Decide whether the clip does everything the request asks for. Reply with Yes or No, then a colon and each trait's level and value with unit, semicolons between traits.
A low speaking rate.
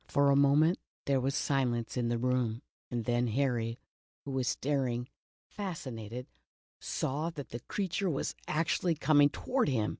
No: average, 150 wpm